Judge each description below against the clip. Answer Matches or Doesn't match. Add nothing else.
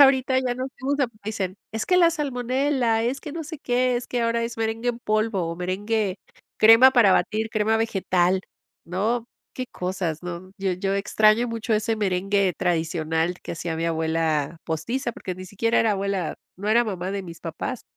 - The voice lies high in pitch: Matches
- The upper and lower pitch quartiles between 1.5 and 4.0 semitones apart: Doesn't match